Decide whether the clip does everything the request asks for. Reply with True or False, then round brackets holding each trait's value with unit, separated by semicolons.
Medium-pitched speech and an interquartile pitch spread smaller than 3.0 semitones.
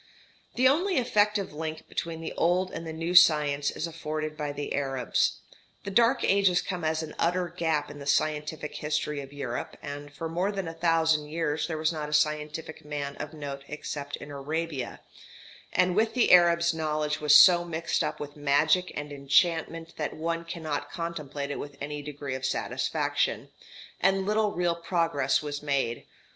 True (155 Hz; 2.6 semitones)